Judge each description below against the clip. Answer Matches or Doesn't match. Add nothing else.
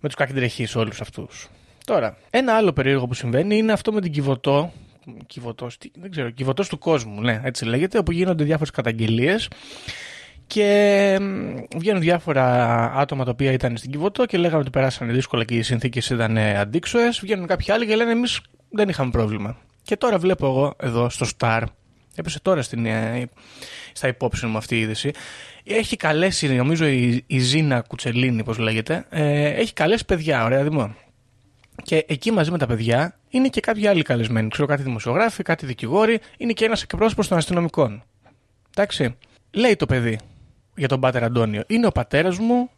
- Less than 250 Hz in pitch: Matches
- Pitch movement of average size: Doesn't match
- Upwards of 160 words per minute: Matches